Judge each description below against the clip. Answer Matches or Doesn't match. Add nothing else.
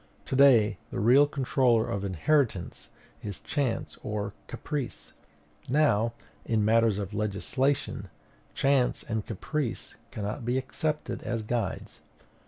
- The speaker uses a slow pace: Matches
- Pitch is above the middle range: Doesn't match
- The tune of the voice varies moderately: Matches